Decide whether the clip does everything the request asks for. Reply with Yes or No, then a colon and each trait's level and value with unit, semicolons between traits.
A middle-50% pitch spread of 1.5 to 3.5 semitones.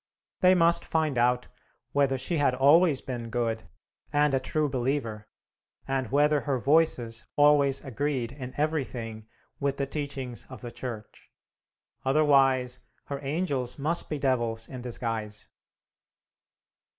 Yes: average, 3.2 semitones